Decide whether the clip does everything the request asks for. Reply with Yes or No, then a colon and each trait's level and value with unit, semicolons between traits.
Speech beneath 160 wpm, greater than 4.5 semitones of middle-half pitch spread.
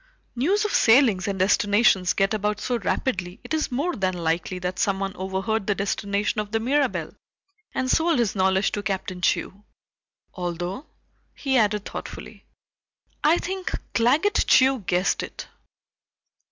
Yes: average, 140 wpm; wide, 5.4 semitones